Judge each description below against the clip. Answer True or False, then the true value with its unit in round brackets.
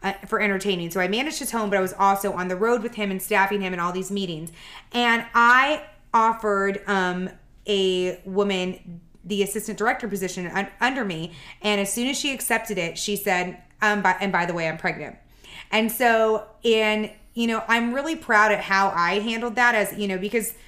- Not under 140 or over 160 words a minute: False (205 wpm)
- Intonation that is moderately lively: True (3.4 semitones)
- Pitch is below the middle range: False (205 Hz)